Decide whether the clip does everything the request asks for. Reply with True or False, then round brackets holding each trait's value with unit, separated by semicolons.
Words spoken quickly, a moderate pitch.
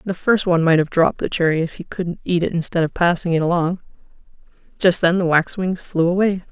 True (220 wpm; 175 Hz)